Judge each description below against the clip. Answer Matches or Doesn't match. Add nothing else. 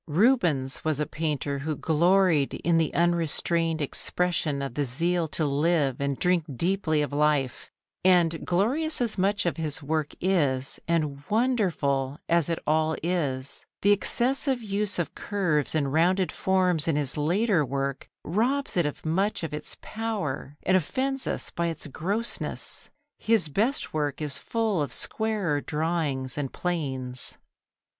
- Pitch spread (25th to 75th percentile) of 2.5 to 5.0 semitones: Matches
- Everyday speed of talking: Matches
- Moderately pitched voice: Matches